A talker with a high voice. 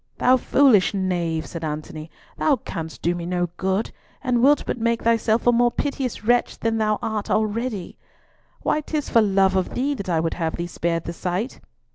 Yes: high, 210 Hz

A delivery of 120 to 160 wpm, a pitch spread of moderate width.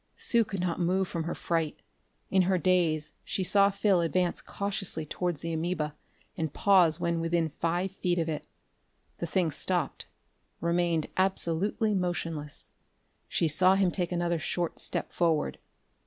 No: average, 150 wpm; narrow, 2.2 semitones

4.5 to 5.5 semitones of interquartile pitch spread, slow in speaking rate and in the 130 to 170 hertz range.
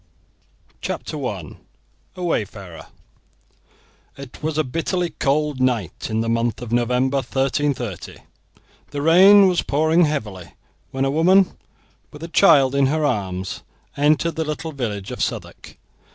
Yes: average, 5.0 semitones; slow, 130 wpm; medium, 140 Hz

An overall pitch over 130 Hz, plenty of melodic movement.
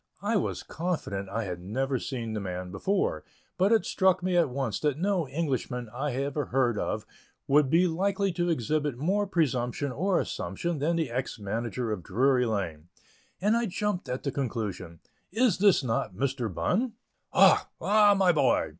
Yes: medium, 140 Hz; wide, 7.7 semitones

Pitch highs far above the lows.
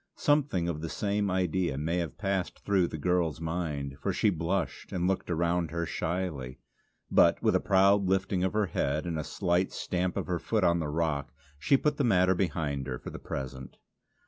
No: average, 3.3 semitones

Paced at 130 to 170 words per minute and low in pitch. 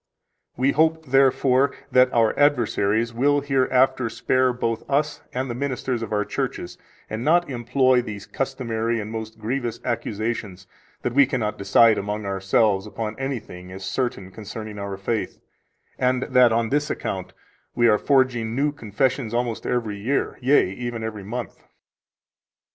Yes: average, 150 wpm; low, 120 Hz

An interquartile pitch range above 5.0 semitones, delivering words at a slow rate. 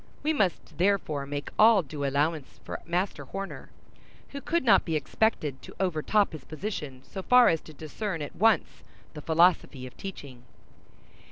No: wide, 5.6 semitones; average, 160 wpm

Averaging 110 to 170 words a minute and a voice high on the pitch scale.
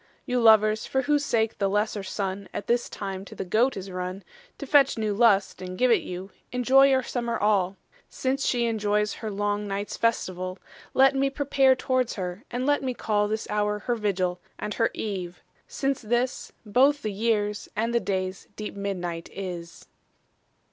No: average, 180 wpm; high, 210 Hz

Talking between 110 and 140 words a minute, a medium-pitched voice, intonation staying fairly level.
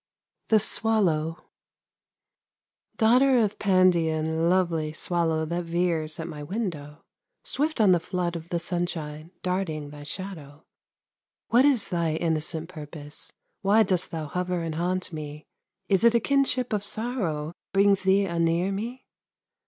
No: slow, 135 wpm; medium, 175 Hz; average, 4.0 semitones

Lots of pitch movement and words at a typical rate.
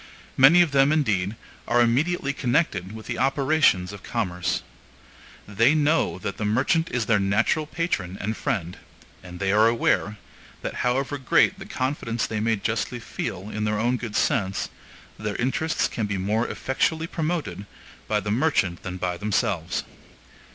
Yes: wide, 5.7 semitones; average, 160 wpm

